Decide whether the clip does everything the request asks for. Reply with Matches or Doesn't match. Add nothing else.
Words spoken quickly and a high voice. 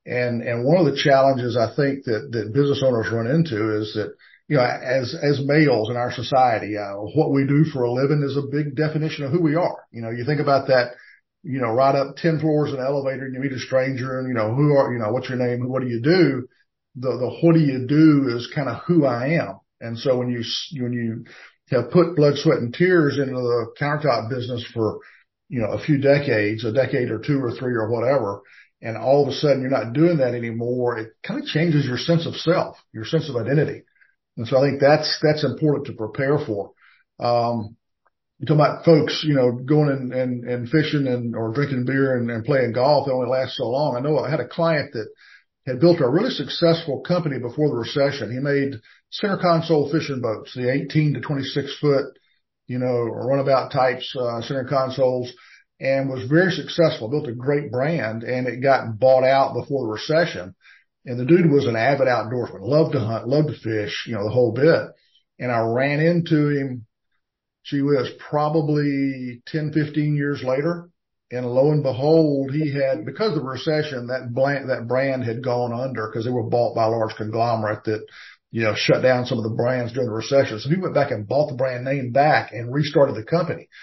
Doesn't match